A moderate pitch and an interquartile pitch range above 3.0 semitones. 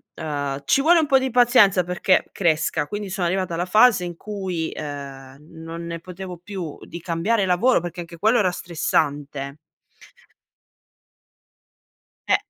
Yes: medium, 175 Hz; average, 3.9 semitones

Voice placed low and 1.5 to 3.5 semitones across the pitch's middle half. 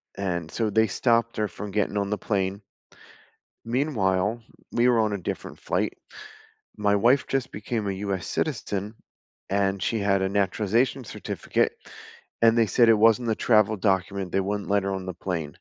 Yes: low, 105 Hz; average, 2.8 semitones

